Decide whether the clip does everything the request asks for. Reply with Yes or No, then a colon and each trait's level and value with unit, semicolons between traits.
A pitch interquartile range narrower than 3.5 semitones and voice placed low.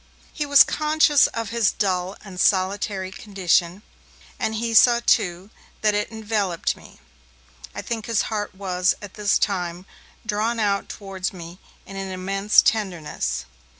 No: average, 3.0 semitones; high, 200 Hz